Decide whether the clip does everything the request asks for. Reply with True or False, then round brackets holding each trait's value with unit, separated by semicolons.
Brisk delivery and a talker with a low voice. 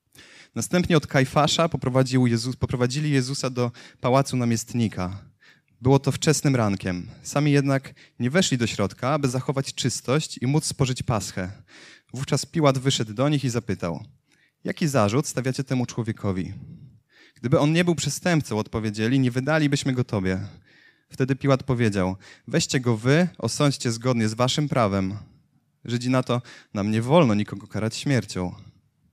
False (140 wpm; 130 Hz)